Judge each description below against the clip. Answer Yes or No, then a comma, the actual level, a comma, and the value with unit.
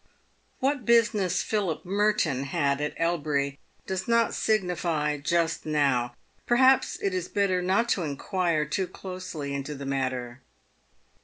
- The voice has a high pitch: No, medium, 170 Hz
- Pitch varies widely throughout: Yes, wide, 5.7 semitones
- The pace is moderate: No, slow, 130 wpm